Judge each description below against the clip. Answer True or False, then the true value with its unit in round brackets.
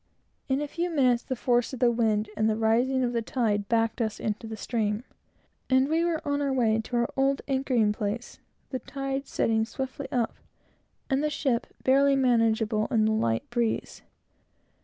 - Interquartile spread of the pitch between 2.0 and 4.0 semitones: True (3.4 semitones)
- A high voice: True (240 Hz)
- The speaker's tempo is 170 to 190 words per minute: True (180 wpm)